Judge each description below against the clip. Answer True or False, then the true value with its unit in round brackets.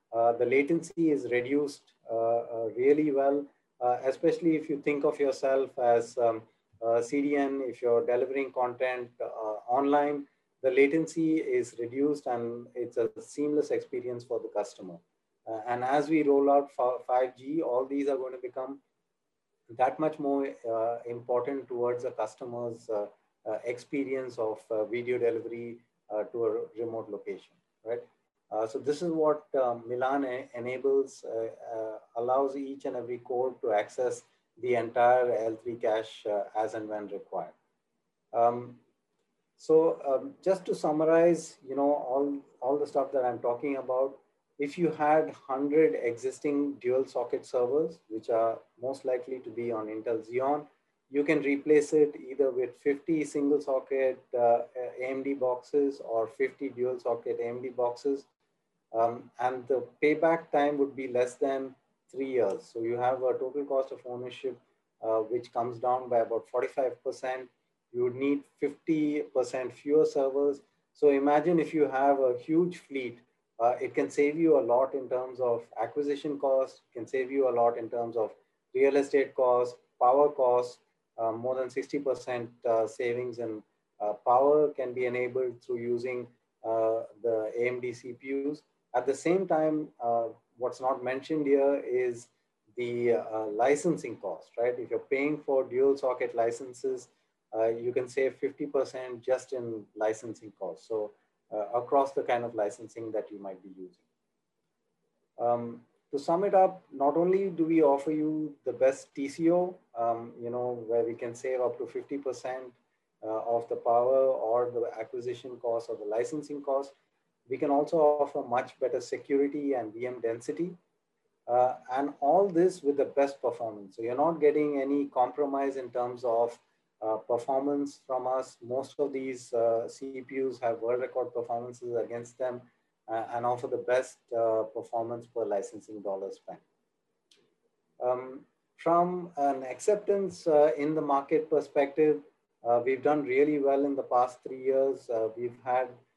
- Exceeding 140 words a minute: True (160 wpm)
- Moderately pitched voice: False (130 Hz)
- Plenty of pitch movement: False (3.4 semitones)